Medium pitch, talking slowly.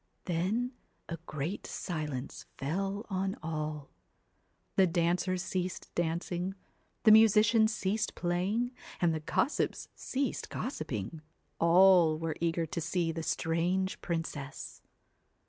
Yes: medium, 175 Hz; slow, 110 wpm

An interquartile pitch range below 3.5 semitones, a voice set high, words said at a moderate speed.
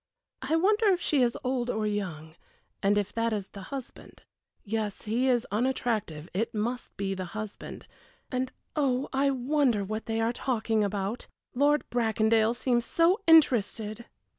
No: average, 3.9 semitones; high, 230 Hz; average, 155 wpm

